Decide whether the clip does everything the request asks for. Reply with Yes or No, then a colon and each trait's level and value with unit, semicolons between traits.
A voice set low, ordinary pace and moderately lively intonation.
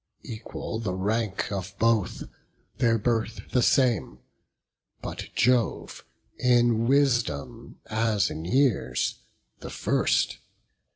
No: low, 115 Hz; slow, 100 wpm; average, 3.4 semitones